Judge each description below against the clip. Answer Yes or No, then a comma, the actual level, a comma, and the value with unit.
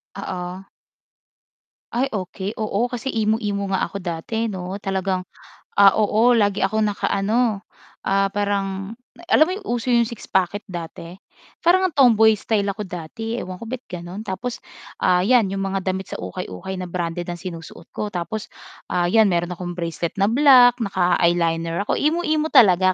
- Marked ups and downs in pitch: No, average, 3.8 semitones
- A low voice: No, high, 195 Hz